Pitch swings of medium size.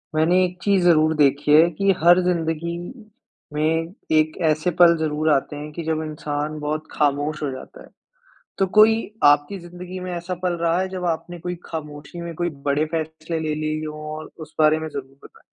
No: narrow, 2.3 semitones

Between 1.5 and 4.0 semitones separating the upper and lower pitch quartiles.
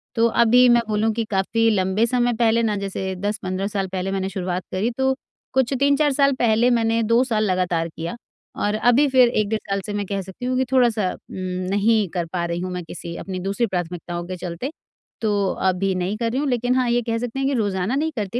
No: average, 4.4 semitones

